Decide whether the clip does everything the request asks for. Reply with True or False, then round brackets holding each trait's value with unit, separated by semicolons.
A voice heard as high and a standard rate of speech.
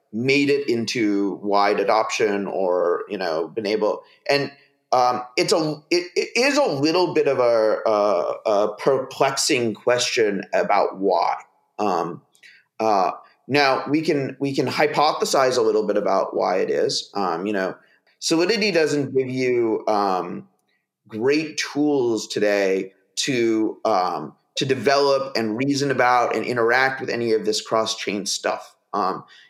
False (135 Hz; 145 wpm)